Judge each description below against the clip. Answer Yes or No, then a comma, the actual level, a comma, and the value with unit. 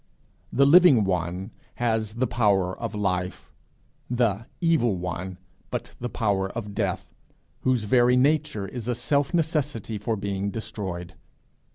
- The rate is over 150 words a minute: No, slow, 135 wpm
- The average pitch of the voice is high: No, low, 110 Hz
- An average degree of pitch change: Yes, average, 4.6 semitones